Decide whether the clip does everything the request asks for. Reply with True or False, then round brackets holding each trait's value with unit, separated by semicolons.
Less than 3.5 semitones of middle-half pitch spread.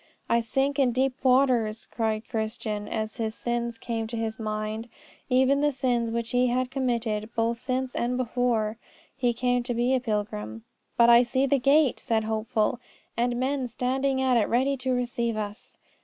True (2.5 semitones)